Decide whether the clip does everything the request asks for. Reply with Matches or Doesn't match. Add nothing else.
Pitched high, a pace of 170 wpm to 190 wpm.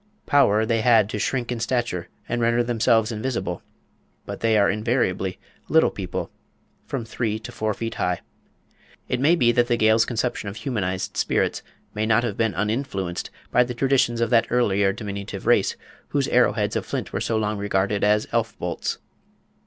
Doesn't match